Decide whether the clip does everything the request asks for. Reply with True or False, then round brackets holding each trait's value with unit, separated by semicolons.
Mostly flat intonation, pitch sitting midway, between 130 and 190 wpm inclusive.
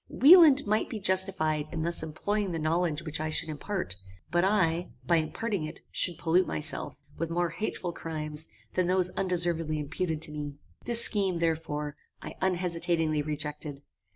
False (3.2 semitones; 165 Hz; 155 wpm)